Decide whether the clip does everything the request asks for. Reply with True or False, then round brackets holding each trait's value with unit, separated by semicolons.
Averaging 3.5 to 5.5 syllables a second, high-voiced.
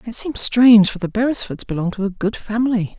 False (5.9 syllables/s; 215 Hz)